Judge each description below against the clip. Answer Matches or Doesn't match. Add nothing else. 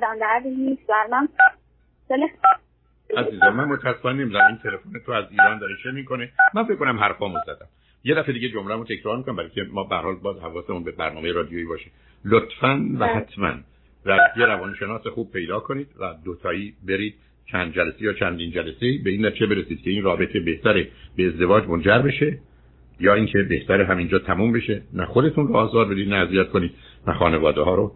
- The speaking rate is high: Matches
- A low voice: Matches